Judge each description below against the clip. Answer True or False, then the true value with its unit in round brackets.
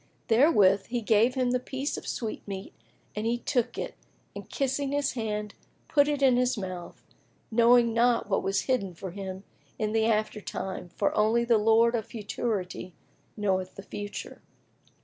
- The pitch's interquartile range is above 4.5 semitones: False (3.5 semitones)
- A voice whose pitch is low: False (225 Hz)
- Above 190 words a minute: False (165 wpm)